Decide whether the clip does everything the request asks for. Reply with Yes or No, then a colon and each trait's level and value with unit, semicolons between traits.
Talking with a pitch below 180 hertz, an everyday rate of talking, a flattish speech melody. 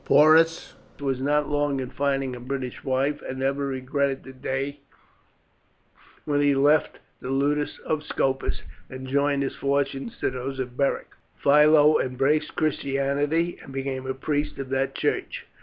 Yes: medium, 140 Hz; average, 150 wpm; narrow, 1.6 semitones